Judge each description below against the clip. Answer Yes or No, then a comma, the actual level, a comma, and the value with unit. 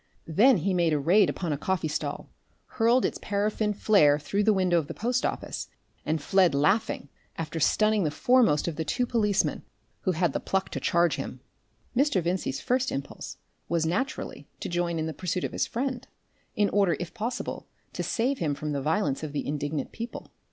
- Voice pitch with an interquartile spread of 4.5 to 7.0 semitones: Yes, wide, 5.5 semitones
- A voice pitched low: No, medium, 180 Hz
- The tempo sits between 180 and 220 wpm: Yes, average, 195 wpm